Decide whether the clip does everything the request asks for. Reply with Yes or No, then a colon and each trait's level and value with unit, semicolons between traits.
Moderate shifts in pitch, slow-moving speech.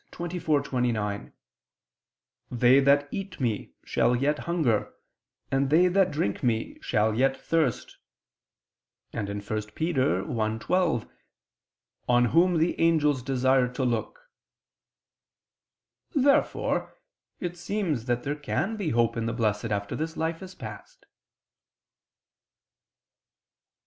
No: wide, 6.2 semitones; slow, 110 wpm